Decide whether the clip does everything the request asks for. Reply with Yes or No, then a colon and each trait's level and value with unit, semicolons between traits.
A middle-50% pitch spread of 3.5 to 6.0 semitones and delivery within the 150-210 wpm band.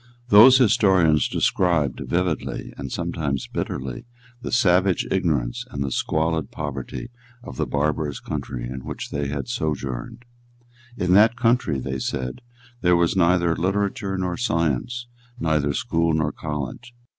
No: average, 5.2 semitones; slow, 135 wpm